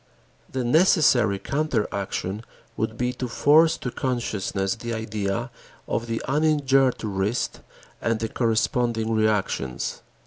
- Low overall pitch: Yes, low, 115 Hz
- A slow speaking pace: Yes, slow, 115 wpm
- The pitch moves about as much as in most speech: Yes, average, 3.3 semitones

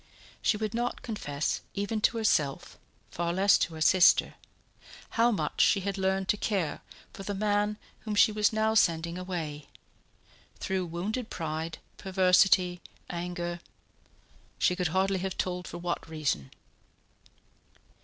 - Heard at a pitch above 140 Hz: Yes, medium, 185 Hz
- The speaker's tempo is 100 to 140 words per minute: Yes, slow, 135 wpm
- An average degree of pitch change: Yes, average, 3.3 semitones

